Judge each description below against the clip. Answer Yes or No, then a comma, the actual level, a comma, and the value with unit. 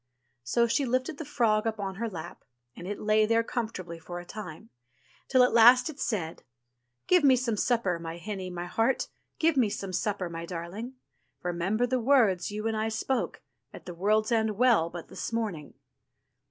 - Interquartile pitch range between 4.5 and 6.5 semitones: Yes, average, 4.9 semitones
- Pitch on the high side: Yes, high, 215 Hz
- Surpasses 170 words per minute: Yes, average, 190 wpm